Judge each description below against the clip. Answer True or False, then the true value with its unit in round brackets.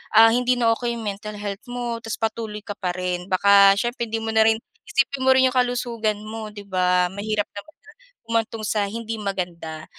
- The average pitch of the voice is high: True (220 Hz)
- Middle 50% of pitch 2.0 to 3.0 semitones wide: True (2.7 semitones)